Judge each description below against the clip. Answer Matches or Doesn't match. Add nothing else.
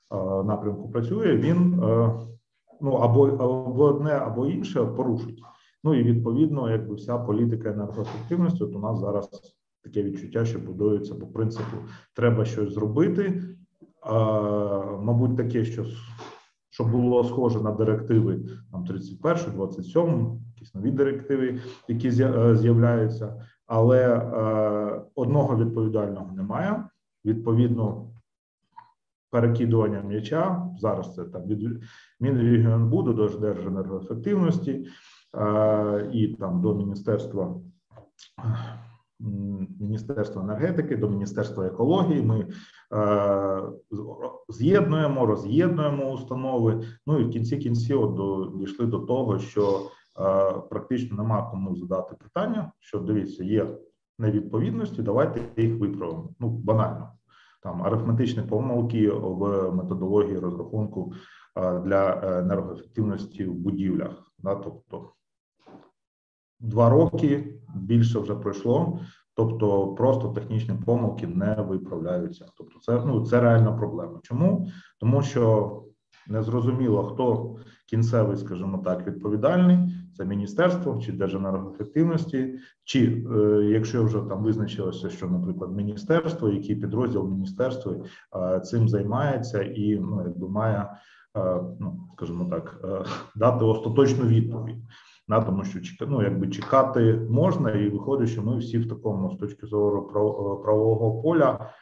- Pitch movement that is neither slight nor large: Matches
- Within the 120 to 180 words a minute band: Doesn't match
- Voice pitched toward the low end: Matches